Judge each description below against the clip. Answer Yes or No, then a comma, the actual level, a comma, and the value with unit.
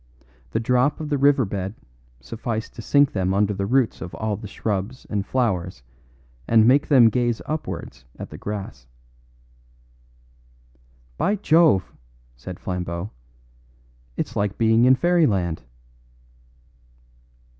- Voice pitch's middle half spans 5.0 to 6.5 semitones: Yes, average, 5.3 semitones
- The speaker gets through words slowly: Yes, slow, 120 wpm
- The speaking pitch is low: Yes, low, 110 Hz